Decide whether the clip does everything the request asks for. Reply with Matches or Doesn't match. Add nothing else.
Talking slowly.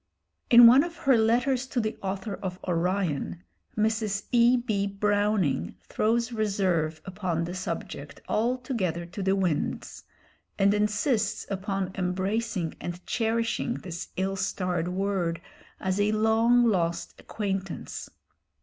Matches